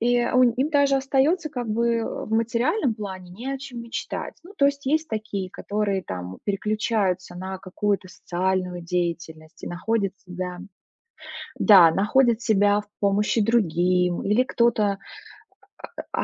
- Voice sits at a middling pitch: No, high, 210 Hz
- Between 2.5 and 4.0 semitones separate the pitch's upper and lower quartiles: No, average, 4.6 semitones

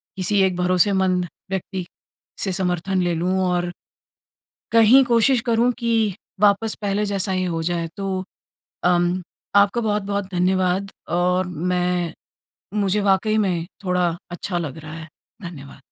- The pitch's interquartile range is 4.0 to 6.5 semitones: No, narrow, 2.4 semitones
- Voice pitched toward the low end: No, medium, 185 Hz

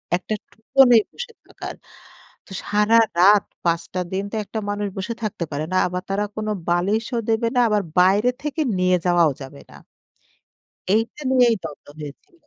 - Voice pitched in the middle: No, high, 205 Hz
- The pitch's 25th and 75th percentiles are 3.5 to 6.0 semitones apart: Yes, average, 3.9 semitones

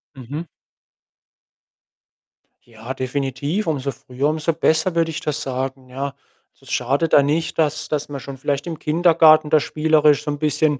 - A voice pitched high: No, medium, 150 Hz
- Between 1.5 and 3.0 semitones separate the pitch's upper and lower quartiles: Yes, average, 2.7 semitones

